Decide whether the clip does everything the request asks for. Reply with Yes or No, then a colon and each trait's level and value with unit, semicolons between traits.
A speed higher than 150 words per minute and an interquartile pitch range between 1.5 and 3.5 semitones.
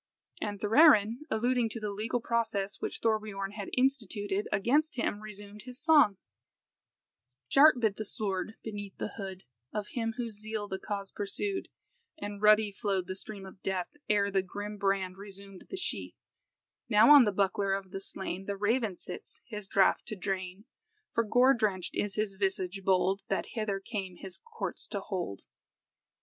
Yes: average, 165 wpm; narrow, 2.4 semitones